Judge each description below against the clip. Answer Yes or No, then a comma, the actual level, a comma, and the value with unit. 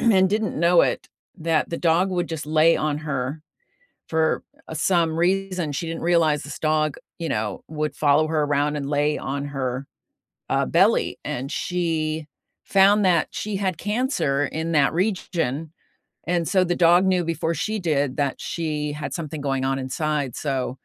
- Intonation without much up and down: No, average, 3.2 semitones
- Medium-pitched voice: Yes, medium, 160 Hz